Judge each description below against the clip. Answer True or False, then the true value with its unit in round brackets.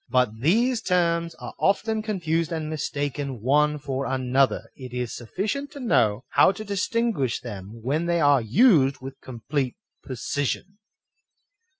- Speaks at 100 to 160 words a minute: True (140 wpm)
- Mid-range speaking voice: True (145 Hz)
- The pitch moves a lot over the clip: True (6.5 semitones)